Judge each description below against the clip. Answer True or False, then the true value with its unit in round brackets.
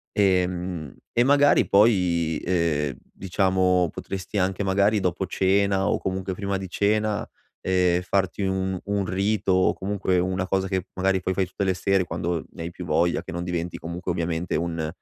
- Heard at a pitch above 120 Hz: False (95 Hz)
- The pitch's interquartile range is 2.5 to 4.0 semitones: False (1.9 semitones)